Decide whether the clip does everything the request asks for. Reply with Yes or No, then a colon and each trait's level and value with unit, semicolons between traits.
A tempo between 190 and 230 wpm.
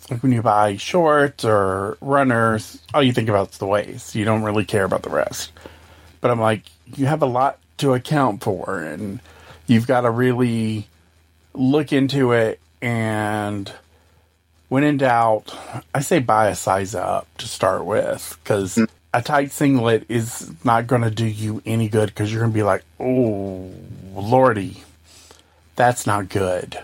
No: average, 165 wpm